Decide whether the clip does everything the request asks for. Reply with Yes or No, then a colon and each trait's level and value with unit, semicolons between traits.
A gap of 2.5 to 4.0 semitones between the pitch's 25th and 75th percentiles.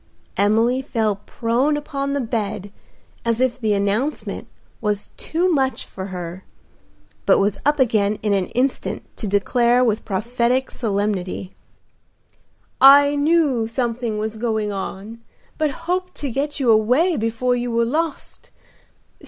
No: average, 4.4 semitones